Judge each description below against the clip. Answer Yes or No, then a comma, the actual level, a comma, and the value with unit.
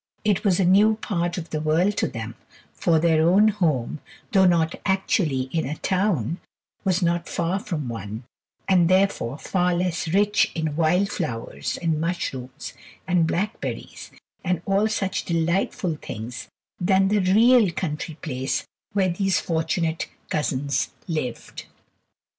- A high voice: No, medium, 170 Hz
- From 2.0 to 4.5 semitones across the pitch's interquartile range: Yes, average, 3.7 semitones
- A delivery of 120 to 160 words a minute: Yes, average, 140 wpm